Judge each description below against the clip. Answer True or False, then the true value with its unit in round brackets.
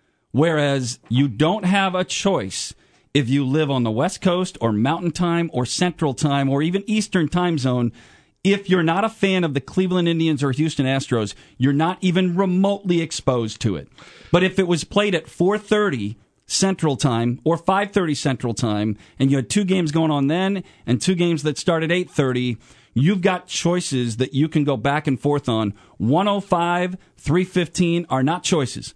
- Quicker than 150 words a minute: True (180 wpm)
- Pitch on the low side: False (155 Hz)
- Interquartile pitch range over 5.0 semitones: True (5.5 semitones)